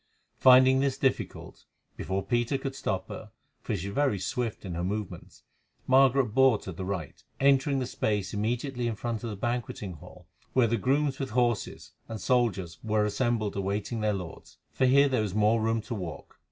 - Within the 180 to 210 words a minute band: Yes, average, 185 wpm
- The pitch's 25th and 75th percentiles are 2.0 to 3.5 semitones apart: No, average, 4.3 semitones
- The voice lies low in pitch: Yes, low, 115 Hz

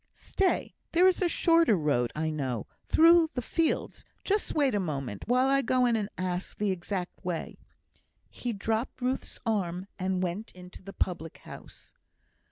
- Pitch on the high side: Yes, high, 205 Hz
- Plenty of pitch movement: Yes, wide, 6.9 semitones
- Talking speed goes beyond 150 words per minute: Yes, average, 165 wpm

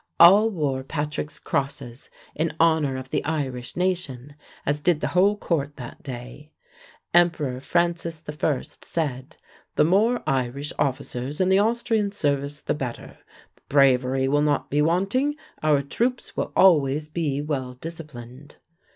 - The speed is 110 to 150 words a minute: Yes, slow, 135 wpm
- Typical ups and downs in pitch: Yes, average, 4.1 semitones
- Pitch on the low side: No, medium, 150 Hz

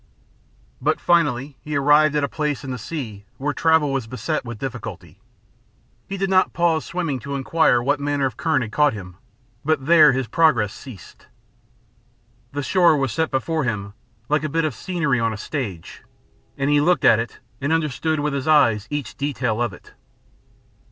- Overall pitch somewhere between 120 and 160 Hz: Yes, medium, 140 Hz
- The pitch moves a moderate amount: Yes, average, 4.2 semitones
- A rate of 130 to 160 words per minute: No, average, 180 wpm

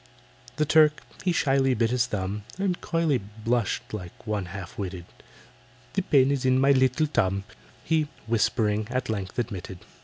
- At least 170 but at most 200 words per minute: No, average, 155 wpm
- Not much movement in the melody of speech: No, wide, 5.4 semitones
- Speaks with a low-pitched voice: Yes, low, 120 Hz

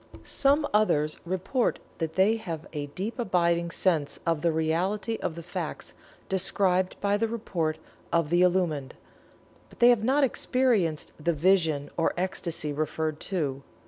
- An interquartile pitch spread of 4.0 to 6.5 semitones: Yes, average, 4.4 semitones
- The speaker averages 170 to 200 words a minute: No, average, 145 wpm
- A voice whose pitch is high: No, medium, 175 Hz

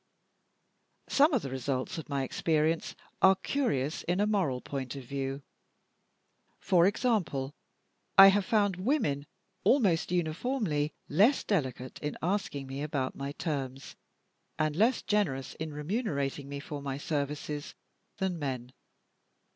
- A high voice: No, medium, 150 Hz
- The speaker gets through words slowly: Yes, slow, 130 wpm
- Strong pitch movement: Yes, wide, 5.9 semitones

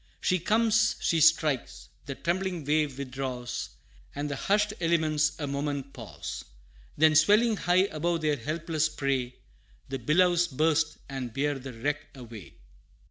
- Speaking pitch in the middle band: Yes, medium, 150 Hz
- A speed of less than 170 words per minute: Yes, slow, 135 wpm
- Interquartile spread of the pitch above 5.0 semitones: No, average, 3.9 semitones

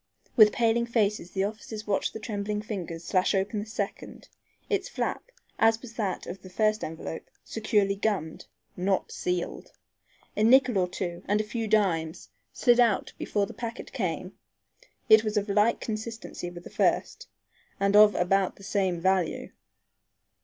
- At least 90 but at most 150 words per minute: No, average, 160 wpm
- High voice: Yes, high, 205 Hz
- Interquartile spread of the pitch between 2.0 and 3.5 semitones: Yes, average, 2.9 semitones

